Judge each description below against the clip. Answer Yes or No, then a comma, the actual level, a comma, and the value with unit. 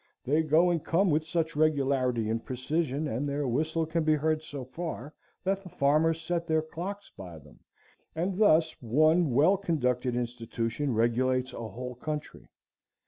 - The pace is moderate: Yes, average, 160 wpm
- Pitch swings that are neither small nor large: Yes, average, 4.4 semitones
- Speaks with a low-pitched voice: No, medium, 150 Hz